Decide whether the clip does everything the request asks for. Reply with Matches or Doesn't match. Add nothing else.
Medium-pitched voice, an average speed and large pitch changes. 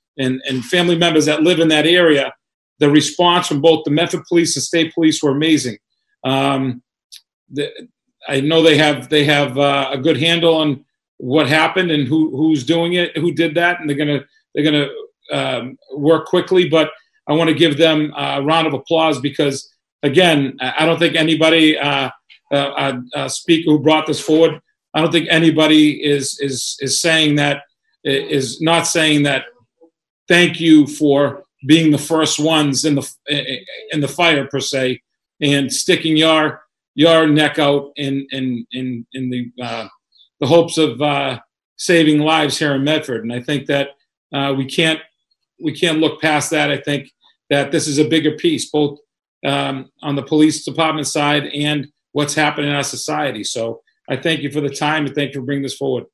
Doesn't match